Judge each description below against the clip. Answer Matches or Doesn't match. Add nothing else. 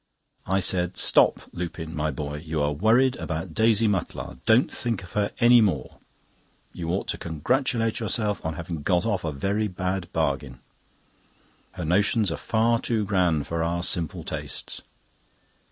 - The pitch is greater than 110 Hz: Doesn't match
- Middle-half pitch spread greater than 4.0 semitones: Matches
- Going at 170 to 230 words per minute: Doesn't match